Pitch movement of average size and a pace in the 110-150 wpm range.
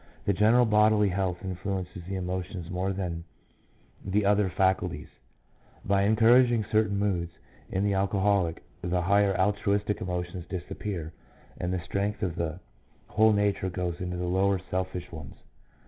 No: narrow, 2.3 semitones; average, 145 wpm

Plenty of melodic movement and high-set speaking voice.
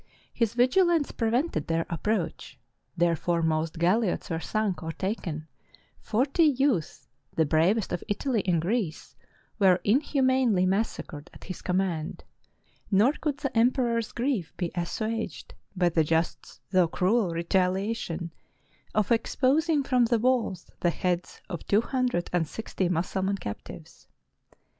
Yes: wide, 5.9 semitones; high, 195 Hz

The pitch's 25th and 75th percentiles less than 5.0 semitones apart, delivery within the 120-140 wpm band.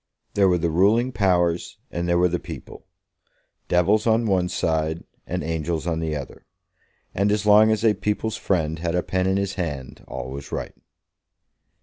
No: average, 3.9 semitones; average, 180 wpm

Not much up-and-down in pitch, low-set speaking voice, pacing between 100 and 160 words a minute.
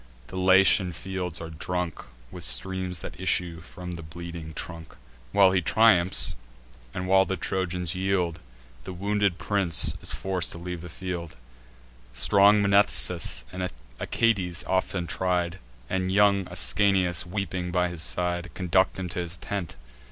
Yes: narrow, 1.6 semitones; very low, 90 Hz; average, 145 wpm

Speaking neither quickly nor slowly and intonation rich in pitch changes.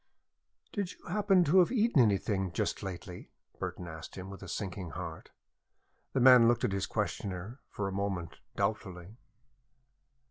Yes: average, 150 wpm; wide, 6.0 semitones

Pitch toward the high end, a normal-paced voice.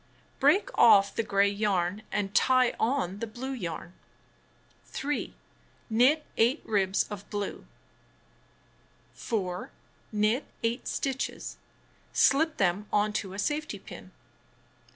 No: high, 215 Hz; slow, 110 wpm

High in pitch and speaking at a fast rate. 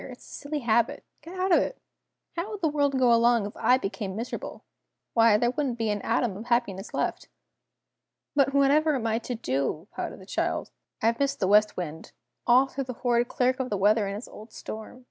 Yes: high, 240 Hz; fast, 210 wpm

